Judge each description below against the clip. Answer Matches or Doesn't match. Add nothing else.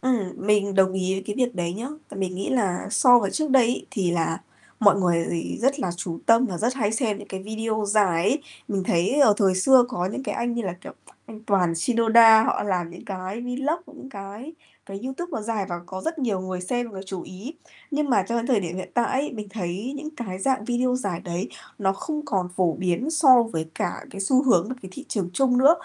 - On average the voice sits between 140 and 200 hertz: Doesn't match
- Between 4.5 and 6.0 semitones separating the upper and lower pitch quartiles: Matches